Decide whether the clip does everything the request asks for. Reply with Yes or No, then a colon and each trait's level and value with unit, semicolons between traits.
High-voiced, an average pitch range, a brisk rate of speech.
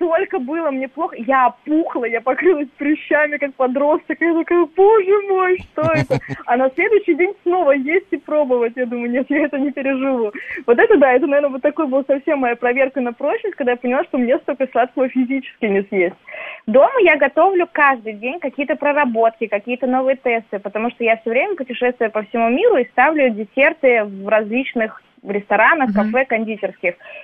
Yes: very high, 270 Hz; average, 4.7 semitones; fast, 180 wpm